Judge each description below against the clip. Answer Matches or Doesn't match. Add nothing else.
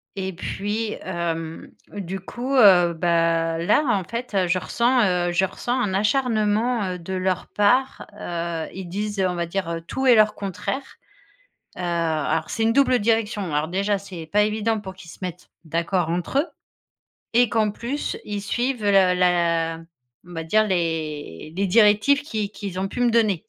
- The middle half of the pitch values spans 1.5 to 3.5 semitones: Doesn't match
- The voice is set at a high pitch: Matches